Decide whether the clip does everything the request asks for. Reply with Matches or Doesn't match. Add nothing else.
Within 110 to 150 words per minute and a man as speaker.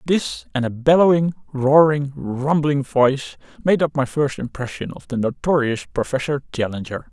Matches